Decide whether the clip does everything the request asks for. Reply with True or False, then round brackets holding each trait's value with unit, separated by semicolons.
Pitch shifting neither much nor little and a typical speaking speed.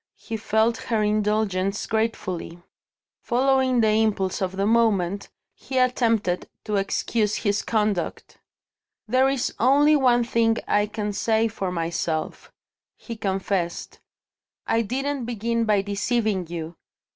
False (3.0 semitones; 120 wpm)